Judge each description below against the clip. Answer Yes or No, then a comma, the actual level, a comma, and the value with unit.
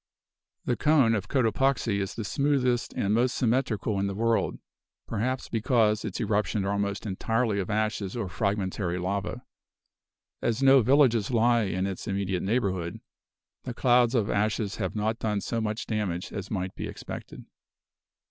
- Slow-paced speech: No, average, 155 wpm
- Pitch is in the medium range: No, low, 110 Hz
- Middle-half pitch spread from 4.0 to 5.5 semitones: No, average, 3.3 semitones